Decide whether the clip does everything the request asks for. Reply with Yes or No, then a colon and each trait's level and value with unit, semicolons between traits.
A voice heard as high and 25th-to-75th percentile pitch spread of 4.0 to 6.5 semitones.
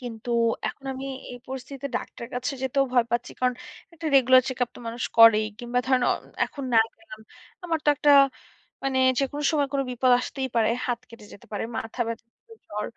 No: very high, 255 Hz; narrow, 2.6 semitones